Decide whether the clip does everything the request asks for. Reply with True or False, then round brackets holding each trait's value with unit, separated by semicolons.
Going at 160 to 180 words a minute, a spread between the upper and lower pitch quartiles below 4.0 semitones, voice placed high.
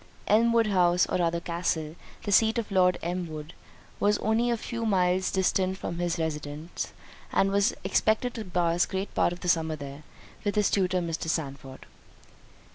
False (170 wpm; 3.6 semitones; 180 Hz)